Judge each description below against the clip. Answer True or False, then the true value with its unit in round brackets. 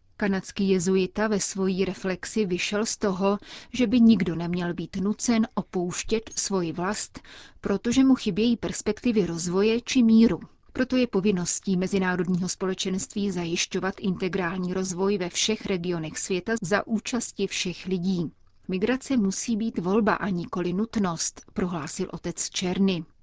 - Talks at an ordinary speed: True (130 wpm)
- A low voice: False (195 Hz)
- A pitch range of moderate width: True (3.0 semitones)